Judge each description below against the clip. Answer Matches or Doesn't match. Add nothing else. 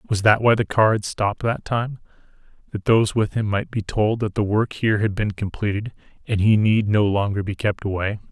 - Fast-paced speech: Matches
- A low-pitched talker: Matches